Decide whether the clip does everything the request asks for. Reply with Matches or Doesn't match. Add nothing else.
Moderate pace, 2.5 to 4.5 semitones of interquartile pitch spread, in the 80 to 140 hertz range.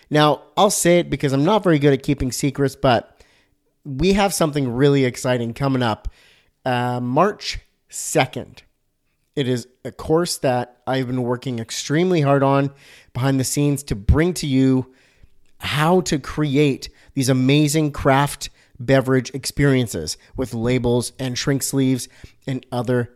Matches